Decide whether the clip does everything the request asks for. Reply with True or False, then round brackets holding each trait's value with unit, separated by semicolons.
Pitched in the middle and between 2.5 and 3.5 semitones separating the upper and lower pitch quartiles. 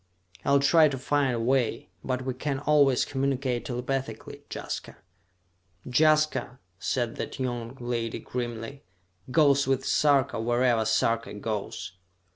False (130 Hz; 2.8 semitones)